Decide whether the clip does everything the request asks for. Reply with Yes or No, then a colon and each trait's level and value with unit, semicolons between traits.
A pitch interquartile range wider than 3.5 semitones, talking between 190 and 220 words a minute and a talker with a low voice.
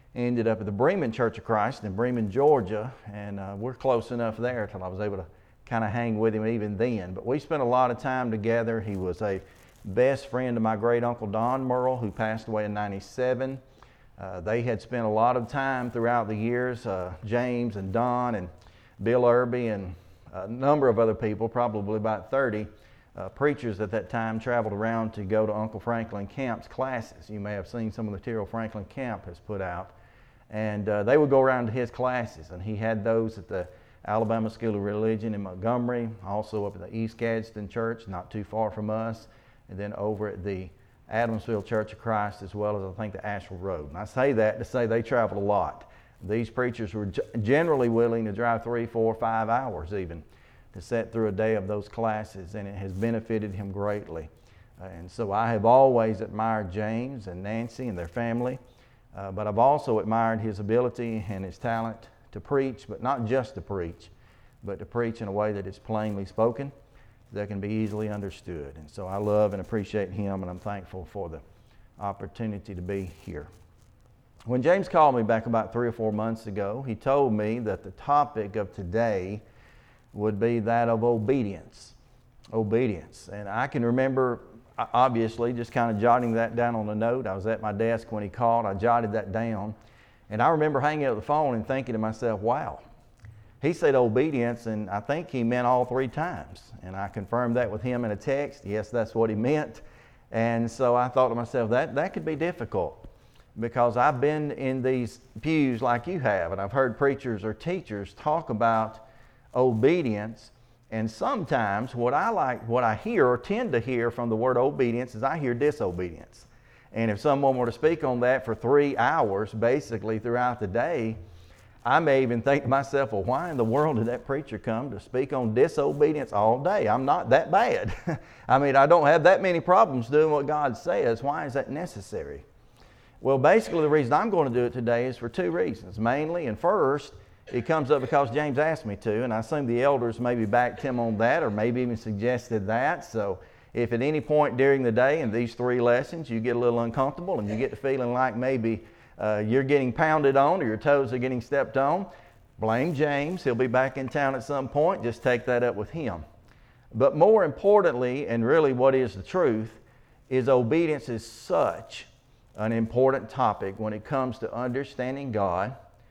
No: average, 3.0 semitones; average, 200 wpm; low, 115 Hz